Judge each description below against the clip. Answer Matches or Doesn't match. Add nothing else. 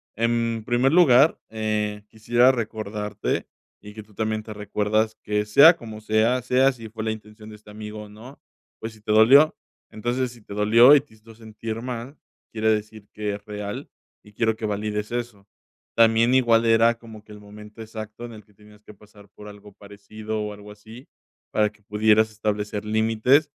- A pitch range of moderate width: Doesn't match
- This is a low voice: Matches